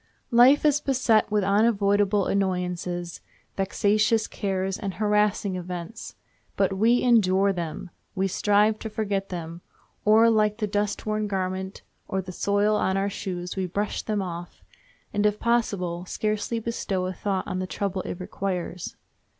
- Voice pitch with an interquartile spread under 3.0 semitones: Yes, narrow, 2.4 semitones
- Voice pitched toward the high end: Yes, high, 200 Hz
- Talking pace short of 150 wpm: Yes, average, 140 wpm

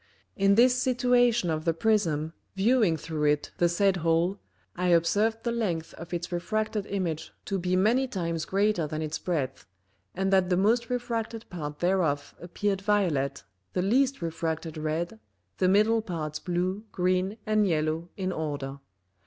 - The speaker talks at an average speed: Yes, average, 155 wpm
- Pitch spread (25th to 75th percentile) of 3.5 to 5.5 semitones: Yes, average, 4.7 semitones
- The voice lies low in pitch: No, medium, 180 Hz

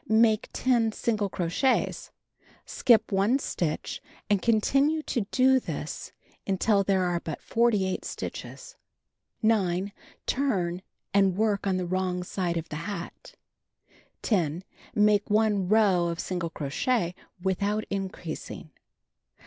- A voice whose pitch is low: No, high, 200 Hz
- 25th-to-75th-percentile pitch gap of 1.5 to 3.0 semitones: No, average, 3.6 semitones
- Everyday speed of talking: No, slow, 115 wpm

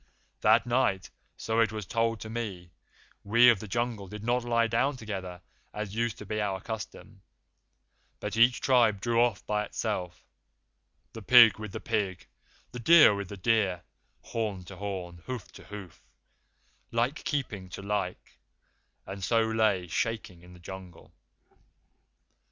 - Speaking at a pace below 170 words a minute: Yes, average, 150 wpm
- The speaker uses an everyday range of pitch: Yes, average, 3.3 semitones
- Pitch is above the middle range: No, low, 105 Hz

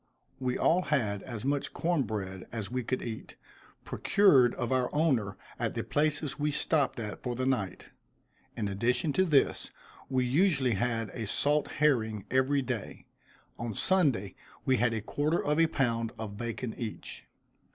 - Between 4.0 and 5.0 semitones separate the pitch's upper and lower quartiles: Yes, average, 4.5 semitones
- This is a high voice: No, low, 125 Hz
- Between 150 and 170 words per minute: Yes, average, 160 wpm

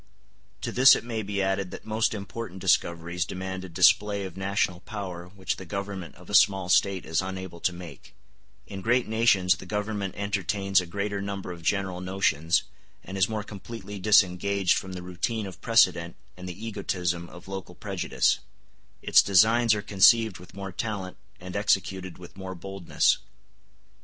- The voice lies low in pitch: Yes, very low, 95 Hz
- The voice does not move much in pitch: Yes, narrow, 2.0 semitones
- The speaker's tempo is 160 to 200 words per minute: Yes, average, 165 wpm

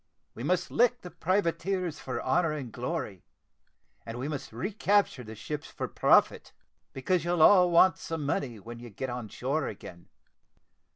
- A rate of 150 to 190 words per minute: Yes, average, 165 wpm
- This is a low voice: No, medium, 150 Hz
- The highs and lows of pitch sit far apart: Yes, wide, 6.6 semitones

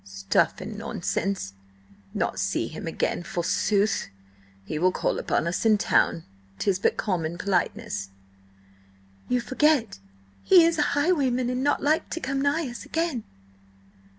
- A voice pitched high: Yes, high, 230 Hz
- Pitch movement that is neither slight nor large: No, wide, 7.7 semitones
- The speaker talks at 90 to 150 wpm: Yes, average, 140 wpm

